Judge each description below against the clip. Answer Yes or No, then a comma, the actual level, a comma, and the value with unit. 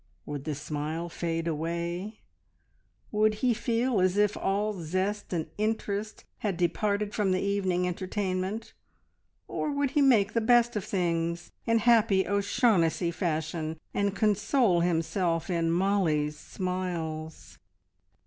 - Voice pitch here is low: No, medium, 185 Hz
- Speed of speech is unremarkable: No, slow, 125 wpm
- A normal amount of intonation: Yes, average, 3.9 semitones